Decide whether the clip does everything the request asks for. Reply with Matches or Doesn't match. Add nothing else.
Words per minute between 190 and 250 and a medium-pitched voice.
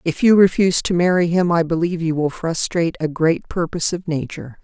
Matches